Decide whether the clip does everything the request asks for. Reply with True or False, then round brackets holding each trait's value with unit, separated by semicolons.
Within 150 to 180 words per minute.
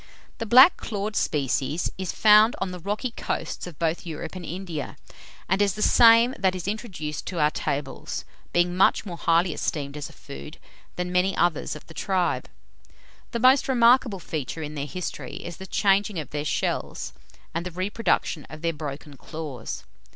True (175 wpm)